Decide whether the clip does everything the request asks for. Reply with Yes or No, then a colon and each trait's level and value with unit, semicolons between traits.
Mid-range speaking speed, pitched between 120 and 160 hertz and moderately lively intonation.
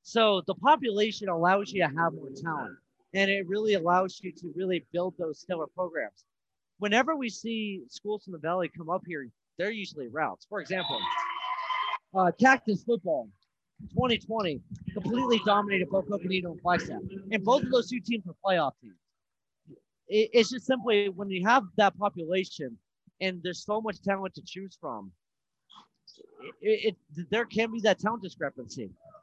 No: average, 160 wpm; high, 195 Hz; average, 4.2 semitones